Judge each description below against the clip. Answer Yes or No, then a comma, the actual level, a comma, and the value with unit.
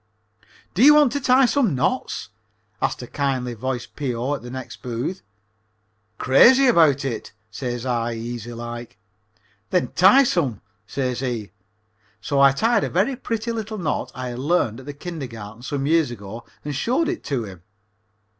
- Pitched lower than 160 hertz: Yes, low, 135 Hz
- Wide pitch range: Yes, wide, 7.9 semitones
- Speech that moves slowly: No, average, 165 wpm